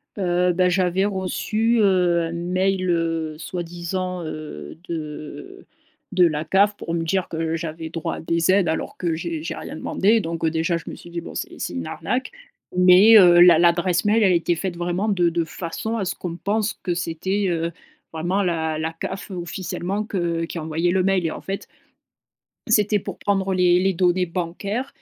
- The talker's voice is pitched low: No, medium, 175 Hz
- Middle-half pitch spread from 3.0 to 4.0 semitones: No, narrow, 2.5 semitones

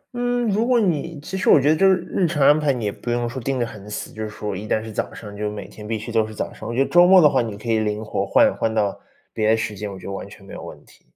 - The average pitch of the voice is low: Yes, low, 115 Hz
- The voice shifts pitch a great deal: Yes, wide, 6.6 semitones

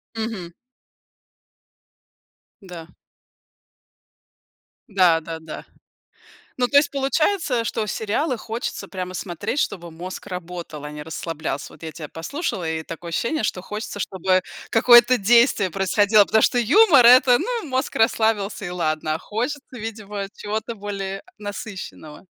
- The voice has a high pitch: Yes, high, 205 Hz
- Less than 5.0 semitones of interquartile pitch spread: No, average, 5.3 semitones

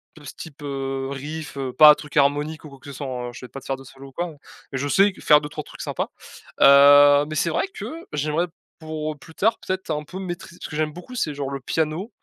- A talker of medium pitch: Yes, medium, 150 Hz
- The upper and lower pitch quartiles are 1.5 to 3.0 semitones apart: Yes, narrow, 2.5 semitones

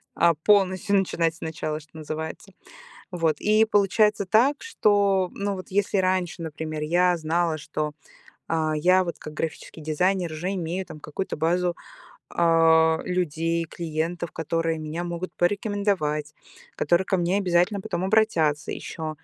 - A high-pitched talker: No, medium, 175 Hz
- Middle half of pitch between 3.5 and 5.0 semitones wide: No, average, 3.1 semitones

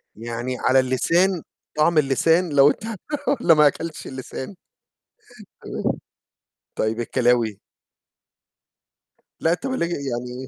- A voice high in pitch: No, low, 135 Hz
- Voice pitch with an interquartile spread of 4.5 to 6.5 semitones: Yes, average, 5.2 semitones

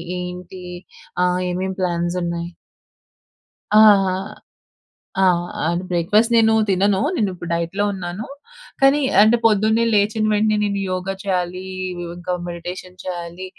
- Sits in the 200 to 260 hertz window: No, medium, 185 Hz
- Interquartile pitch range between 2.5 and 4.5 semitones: Yes, average, 2.9 semitones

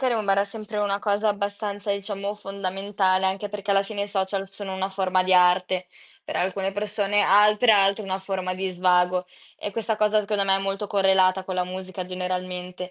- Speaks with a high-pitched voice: Yes, high, 195 Hz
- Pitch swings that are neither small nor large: No, narrow, 1.6 semitones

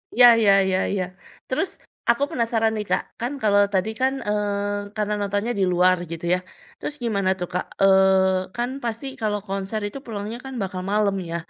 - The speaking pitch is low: No, high, 205 Hz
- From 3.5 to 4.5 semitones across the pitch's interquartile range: No, average, 2.7 semitones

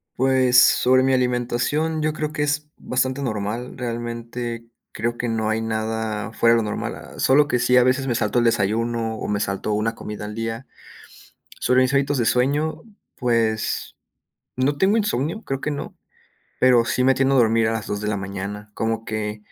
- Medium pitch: No, low, 120 Hz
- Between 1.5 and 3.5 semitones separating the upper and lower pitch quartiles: Yes, average, 2.9 semitones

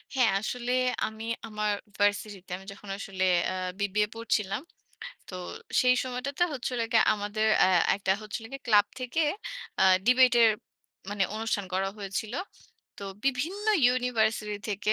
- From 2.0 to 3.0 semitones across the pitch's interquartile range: No, average, 3.4 semitones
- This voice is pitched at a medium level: No, high, 215 Hz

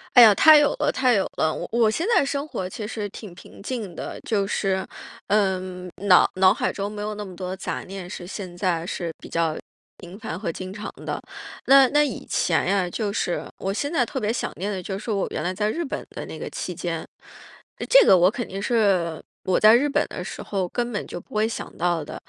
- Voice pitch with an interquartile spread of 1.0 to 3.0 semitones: No, average, 3.7 semitones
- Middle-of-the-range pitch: No, high, 200 Hz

